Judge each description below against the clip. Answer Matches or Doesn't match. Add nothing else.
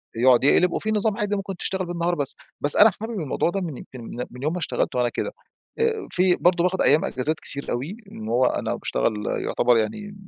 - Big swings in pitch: Matches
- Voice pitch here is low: Doesn't match